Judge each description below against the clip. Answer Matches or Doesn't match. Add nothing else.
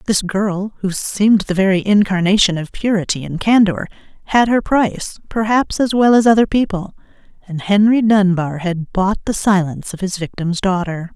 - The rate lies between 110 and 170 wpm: Matches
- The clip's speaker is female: Matches